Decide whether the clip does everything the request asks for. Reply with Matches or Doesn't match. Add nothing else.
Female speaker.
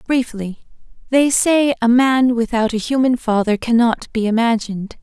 Matches